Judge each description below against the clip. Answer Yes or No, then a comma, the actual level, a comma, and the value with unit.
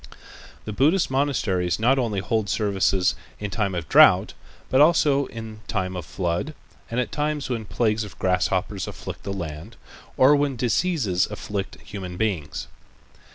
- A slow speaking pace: No, average, 150 wpm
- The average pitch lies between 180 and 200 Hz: No, low, 105 Hz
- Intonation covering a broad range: Yes, wide, 6.0 semitones